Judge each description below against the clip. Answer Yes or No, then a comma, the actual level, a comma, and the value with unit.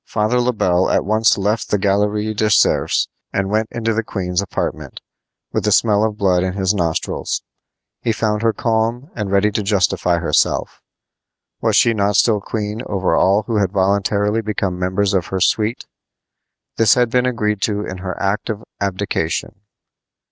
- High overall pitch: No, low, 105 Hz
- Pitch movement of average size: No, narrow, 2.2 semitones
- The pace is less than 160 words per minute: No, average, 170 wpm